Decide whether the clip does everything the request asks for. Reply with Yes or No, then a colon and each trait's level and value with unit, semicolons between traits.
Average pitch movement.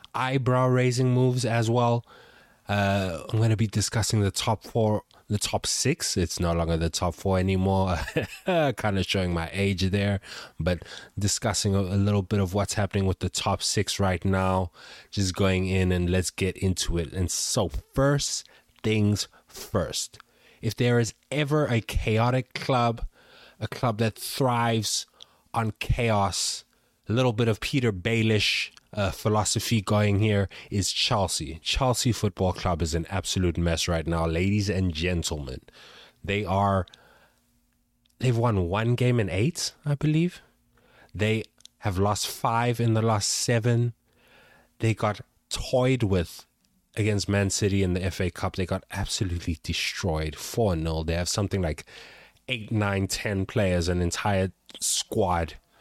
Yes: average, 3.8 semitones